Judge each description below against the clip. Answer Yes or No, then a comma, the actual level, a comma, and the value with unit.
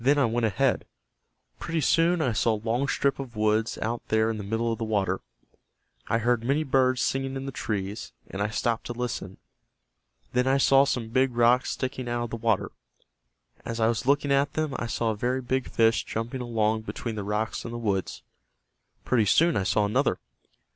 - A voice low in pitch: Yes, low, 120 Hz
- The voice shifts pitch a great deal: No, average, 3.2 semitones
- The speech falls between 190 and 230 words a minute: Yes, average, 200 wpm